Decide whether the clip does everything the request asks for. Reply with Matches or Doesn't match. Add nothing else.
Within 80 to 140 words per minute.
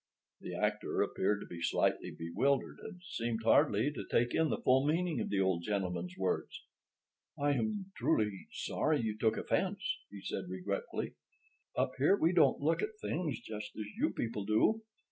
Doesn't match